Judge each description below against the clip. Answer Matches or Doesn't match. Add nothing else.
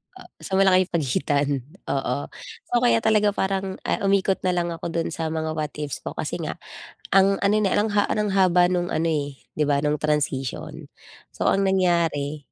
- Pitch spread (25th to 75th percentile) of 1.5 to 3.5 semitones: Doesn't match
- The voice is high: Doesn't match